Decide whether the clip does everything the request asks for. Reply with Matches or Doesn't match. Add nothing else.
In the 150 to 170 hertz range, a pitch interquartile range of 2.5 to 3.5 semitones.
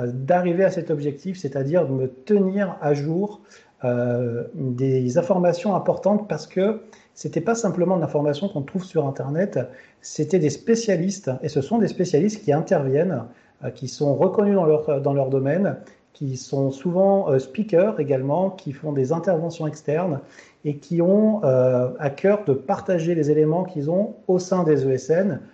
Doesn't match